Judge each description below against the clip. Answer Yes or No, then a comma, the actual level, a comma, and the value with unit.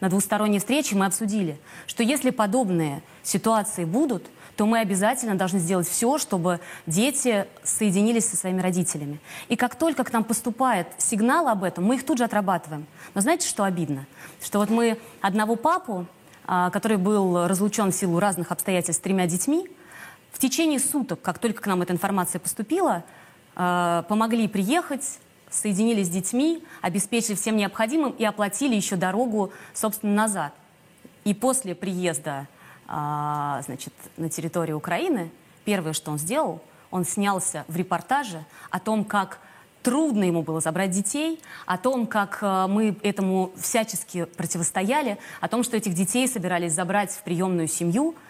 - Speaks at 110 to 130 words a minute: No, average, 150 wpm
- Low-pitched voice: No, high, 200 Hz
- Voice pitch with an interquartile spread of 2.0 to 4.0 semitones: No, average, 4.4 semitones